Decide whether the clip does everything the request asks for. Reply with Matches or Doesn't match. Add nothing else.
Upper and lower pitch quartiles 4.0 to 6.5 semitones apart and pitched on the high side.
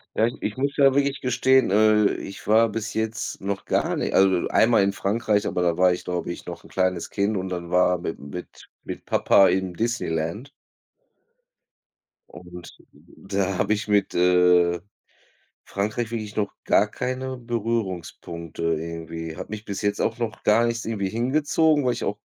Doesn't match